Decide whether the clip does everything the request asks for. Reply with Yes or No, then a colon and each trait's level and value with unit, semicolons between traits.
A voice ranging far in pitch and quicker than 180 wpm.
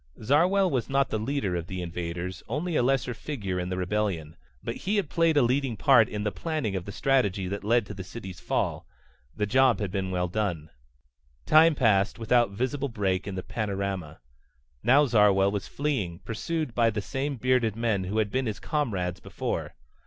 Yes: wide, 5.7 semitones; average, 190 wpm